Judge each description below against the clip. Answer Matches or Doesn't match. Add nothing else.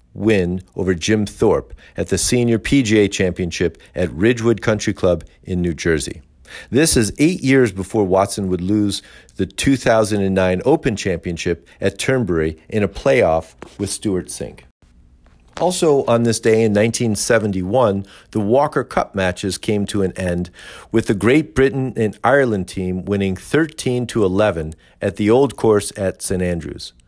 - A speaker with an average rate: Matches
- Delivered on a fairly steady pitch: Doesn't match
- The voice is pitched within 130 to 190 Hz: Doesn't match